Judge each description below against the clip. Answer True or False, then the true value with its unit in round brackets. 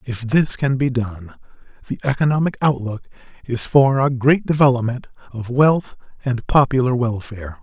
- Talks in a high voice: False (130 Hz)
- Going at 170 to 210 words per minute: False (140 wpm)